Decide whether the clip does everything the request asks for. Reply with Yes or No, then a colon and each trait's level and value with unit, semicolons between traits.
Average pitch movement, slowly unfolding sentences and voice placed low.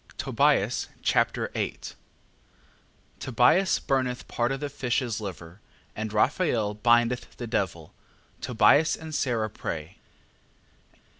Yes: average, 3.9 semitones; slow, 100 wpm; low, 120 Hz